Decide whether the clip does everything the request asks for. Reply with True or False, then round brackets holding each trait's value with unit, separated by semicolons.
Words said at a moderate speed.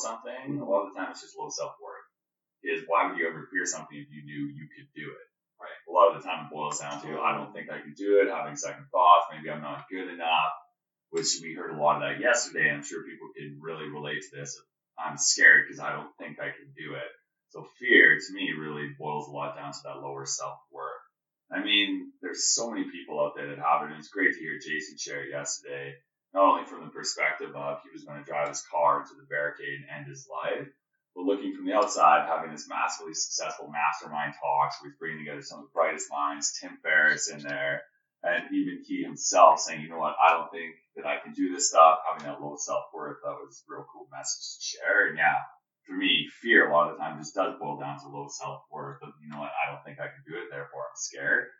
False (250 wpm)